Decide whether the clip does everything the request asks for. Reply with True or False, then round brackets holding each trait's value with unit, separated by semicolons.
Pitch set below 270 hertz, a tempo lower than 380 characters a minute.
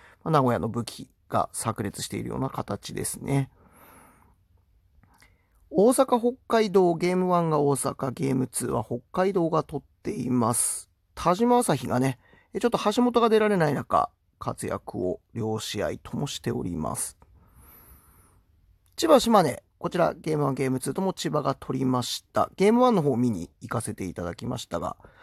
True (135 Hz; 290 characters per minute)